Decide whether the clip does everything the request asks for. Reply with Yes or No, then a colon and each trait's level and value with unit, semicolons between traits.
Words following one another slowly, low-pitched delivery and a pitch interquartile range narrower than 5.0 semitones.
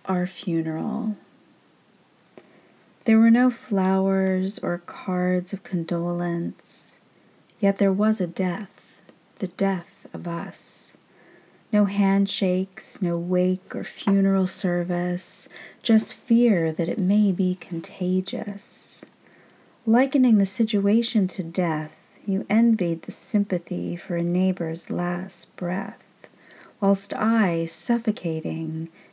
No: slow, 105 wpm; high, 190 Hz; average, 2.9 semitones